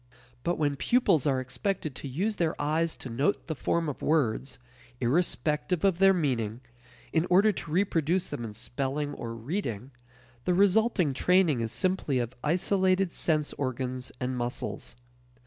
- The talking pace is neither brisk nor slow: Yes, average, 150 wpm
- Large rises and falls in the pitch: Yes, wide, 5.9 semitones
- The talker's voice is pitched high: No, medium, 150 Hz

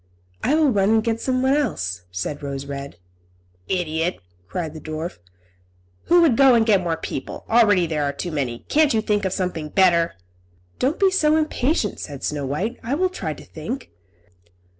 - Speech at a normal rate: Yes, average, 180 wpm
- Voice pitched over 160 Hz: Yes, high, 190 Hz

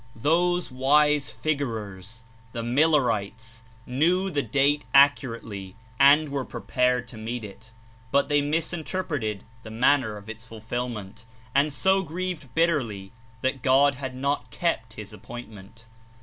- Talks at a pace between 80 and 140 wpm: Yes, slow, 135 wpm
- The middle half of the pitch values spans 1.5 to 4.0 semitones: No, average, 4.7 semitones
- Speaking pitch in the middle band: No, low, 130 Hz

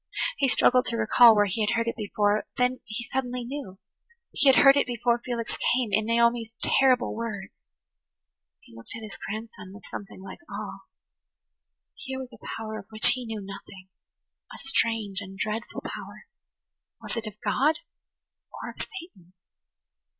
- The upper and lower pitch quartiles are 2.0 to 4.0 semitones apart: Yes, average, 3.2 semitones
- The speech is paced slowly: No, average, 165 wpm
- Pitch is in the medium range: No, high, 225 Hz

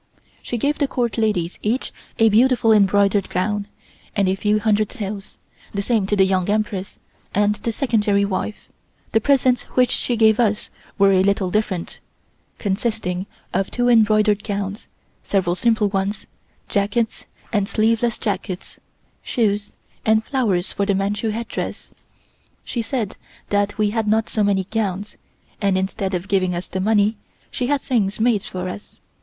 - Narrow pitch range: Yes, narrow, 2.3 semitones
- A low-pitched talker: No, high, 210 Hz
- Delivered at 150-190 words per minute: Yes, average, 155 wpm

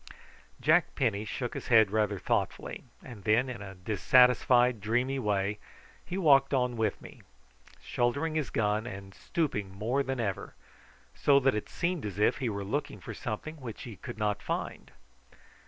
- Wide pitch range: No, average, 4.3 semitones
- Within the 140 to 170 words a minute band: Yes, average, 165 wpm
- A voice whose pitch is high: No, low, 120 Hz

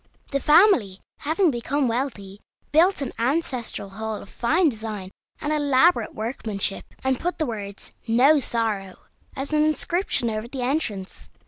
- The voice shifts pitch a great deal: Yes, wide, 5.9 semitones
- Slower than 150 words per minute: Yes, average, 140 wpm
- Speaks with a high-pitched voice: Yes, very high, 250 Hz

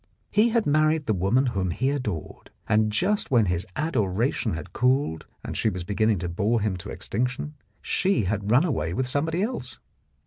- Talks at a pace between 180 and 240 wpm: Yes, average, 185 wpm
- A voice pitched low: Yes, low, 120 Hz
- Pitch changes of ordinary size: No, wide, 6.7 semitones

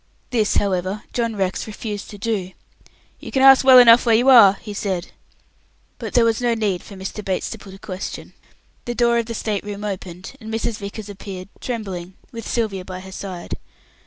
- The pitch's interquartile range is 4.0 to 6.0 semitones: No, average, 3.3 semitones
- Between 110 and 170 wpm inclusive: No, average, 195 wpm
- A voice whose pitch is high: Yes, high, 210 Hz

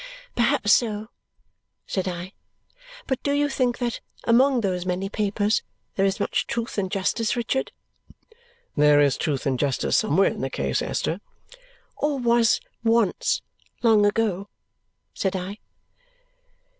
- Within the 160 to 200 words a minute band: No, slow, 135 wpm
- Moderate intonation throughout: Yes, average, 4.4 semitones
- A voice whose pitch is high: Yes, high, 205 Hz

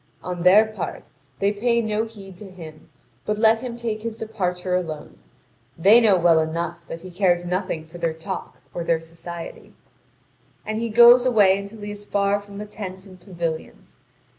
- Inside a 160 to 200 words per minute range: Yes, average, 180 wpm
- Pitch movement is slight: No, average, 3.8 semitones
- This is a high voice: Yes, high, 195 Hz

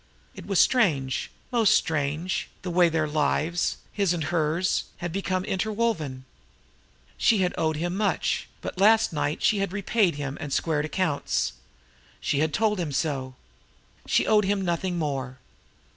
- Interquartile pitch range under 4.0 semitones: No, average, 4.8 semitones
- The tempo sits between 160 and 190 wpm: No, average, 150 wpm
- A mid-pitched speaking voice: Yes, medium, 170 Hz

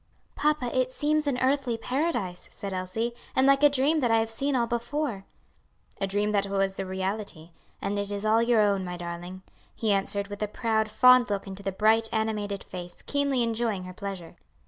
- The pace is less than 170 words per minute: No, average, 195 wpm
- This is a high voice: Yes, high, 215 Hz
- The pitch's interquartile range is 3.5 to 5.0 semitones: Yes, average, 4.3 semitones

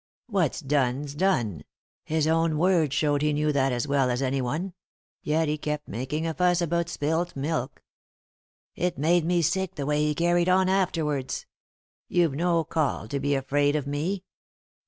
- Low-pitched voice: No, medium, 150 Hz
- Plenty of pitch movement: No, average, 3.4 semitones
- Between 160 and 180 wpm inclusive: Yes, average, 170 wpm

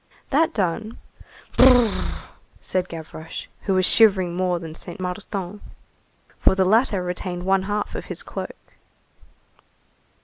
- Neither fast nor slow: No, slow, 125 wpm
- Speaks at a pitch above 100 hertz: Yes, high, 190 Hz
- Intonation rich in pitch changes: No, average, 2.8 semitones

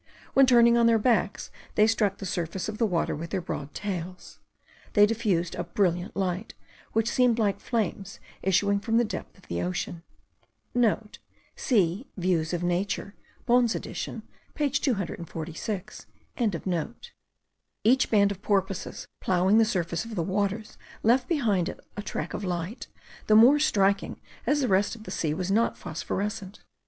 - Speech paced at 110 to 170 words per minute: Yes, average, 155 wpm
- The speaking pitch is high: Yes, high, 200 Hz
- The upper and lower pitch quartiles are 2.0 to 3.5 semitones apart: No, average, 4.0 semitones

